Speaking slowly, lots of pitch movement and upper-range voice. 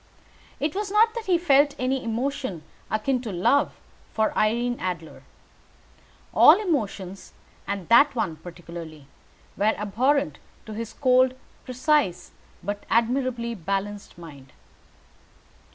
Yes: slow, 115 wpm; wide, 6.0 semitones; high, 230 Hz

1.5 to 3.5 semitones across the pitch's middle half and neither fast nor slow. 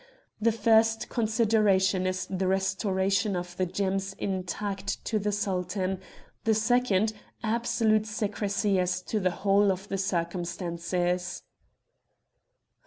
No: narrow, 2.6 semitones; slow, 110 wpm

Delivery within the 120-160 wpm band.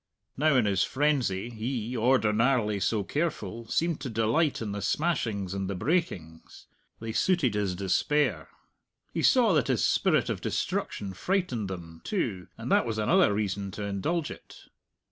Yes: average, 155 wpm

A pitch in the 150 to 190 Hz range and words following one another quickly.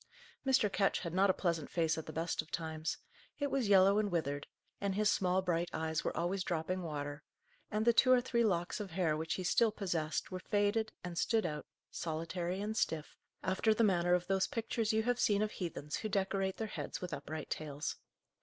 Yes: medium, 185 Hz; fast, 210 wpm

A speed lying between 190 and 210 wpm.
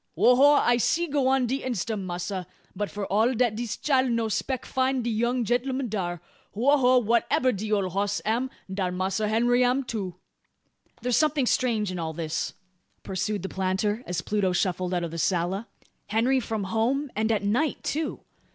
No: average, 180 wpm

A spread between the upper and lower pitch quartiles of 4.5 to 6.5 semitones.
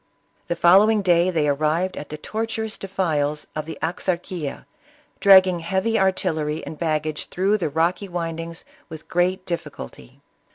No: average, 3.3 semitones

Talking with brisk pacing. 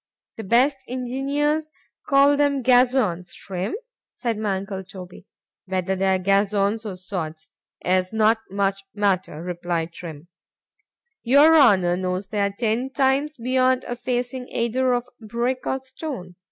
No: slow, 135 wpm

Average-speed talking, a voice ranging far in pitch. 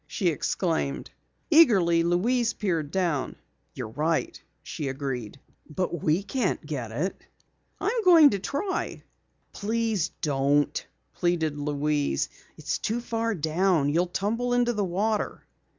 No: slow, 120 wpm; wide, 7.1 semitones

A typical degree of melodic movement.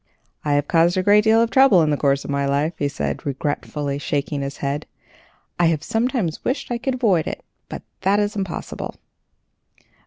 No: wide, 6.6 semitones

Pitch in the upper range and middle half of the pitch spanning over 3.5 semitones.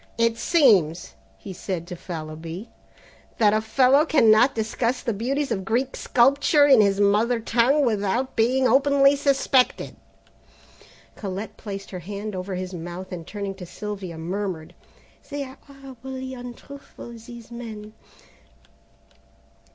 Yes: high, 225 Hz; average, 5.1 semitones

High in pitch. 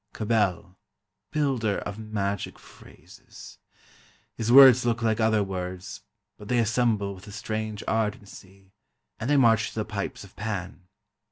No: low, 110 Hz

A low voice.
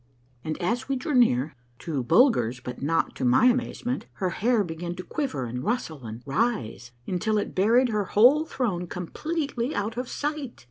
No: high, 210 Hz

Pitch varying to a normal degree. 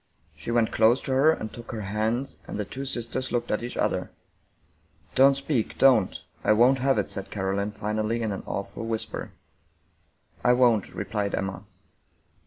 Yes: average, 3.4 semitones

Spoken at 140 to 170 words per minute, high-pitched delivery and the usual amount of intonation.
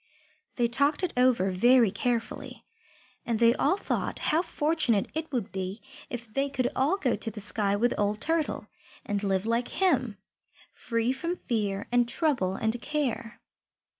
Yes: average, 160 wpm; high, 240 Hz; average, 4.8 semitones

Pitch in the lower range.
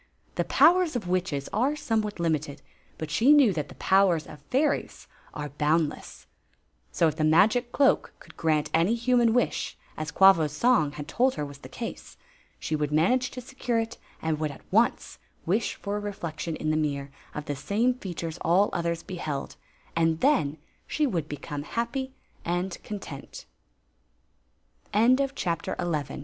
No: medium, 170 Hz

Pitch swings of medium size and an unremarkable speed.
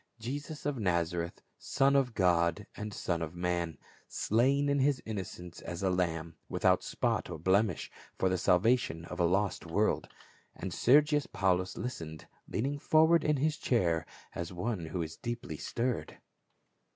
No: wide, 7.0 semitones; average, 150 wpm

